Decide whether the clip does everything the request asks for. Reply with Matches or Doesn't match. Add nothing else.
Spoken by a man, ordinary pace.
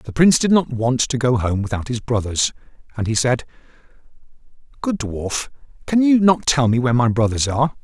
Matches